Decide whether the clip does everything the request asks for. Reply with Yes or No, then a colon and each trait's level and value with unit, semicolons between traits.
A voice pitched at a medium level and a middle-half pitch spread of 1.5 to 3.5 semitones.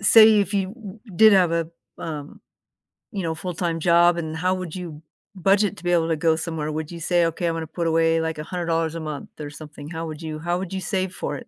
Yes: medium, 165 Hz; narrow, 2.4 semitones